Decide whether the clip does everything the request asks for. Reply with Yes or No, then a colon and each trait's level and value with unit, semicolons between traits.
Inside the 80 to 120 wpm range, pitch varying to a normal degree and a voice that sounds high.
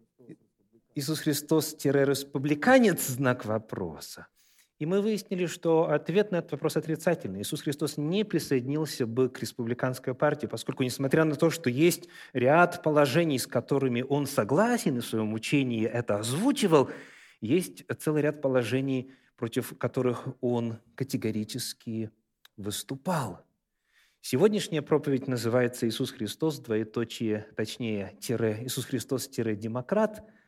No: average, 115 wpm; average, 5.0 semitones; low, 135 Hz